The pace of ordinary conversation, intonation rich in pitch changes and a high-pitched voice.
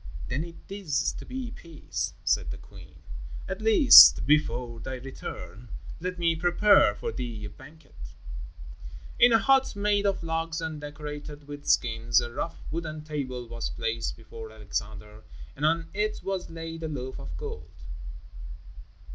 No: average, 150 wpm; wide, 6.6 semitones; medium, 145 Hz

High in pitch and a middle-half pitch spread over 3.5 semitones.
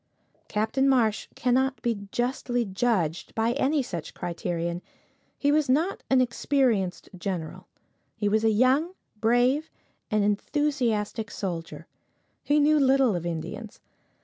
Yes: high, 235 Hz; average, 5.0 semitones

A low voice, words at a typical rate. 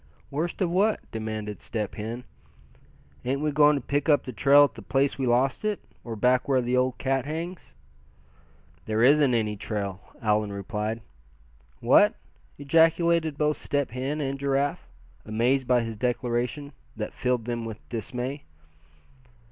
Yes: low, 130 Hz; average, 150 wpm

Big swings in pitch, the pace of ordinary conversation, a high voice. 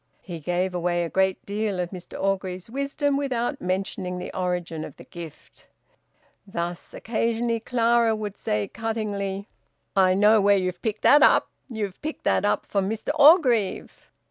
No: average, 4.0 semitones; average, 155 wpm; high, 200 Hz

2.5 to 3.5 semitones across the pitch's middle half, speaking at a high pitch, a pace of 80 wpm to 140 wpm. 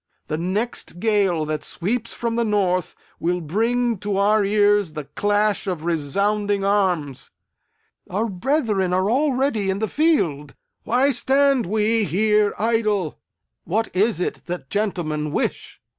No: average, 4.0 semitones; high, 205 Hz; slow, 135 wpm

